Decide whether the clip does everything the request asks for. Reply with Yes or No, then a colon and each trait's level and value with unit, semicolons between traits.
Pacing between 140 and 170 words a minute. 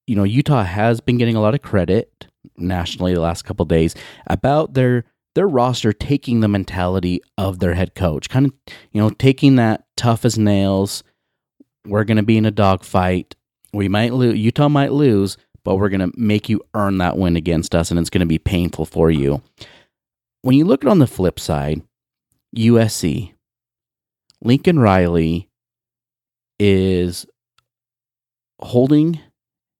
Yes: average, 160 wpm